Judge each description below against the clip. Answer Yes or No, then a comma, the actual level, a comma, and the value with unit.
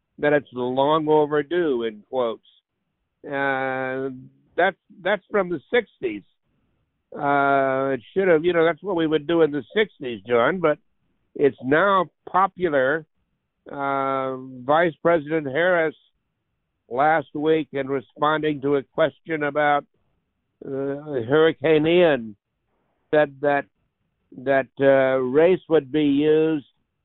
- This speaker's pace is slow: Yes, slow, 120 wpm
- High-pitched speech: No, medium, 150 Hz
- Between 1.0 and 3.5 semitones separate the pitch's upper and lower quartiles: Yes, average, 3.0 semitones